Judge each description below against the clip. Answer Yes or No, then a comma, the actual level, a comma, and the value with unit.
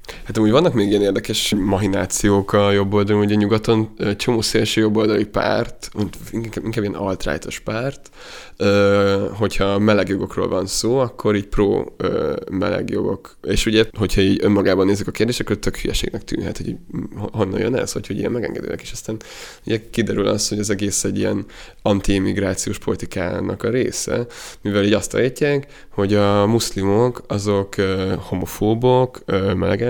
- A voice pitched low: Yes, low, 105 Hz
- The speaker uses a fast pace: No, average, 145 wpm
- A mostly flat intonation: Yes, narrow, 1.9 semitones